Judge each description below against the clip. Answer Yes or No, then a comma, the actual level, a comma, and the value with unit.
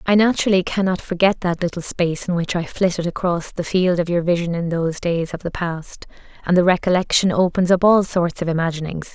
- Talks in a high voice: No, medium, 175 Hz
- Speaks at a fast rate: Yes, fast, 210 wpm